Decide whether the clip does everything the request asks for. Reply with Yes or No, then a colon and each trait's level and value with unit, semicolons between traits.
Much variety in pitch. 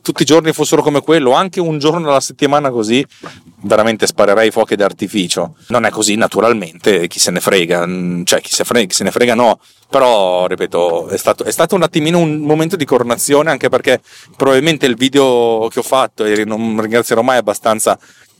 Yes: wide, 6.0 semitones